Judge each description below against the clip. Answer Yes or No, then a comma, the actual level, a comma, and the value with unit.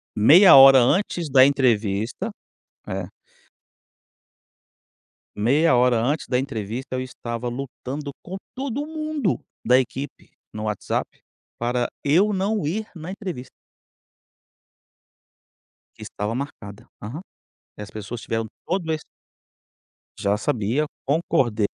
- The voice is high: No, low, 130 Hz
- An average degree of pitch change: No, wide, 6.4 semitones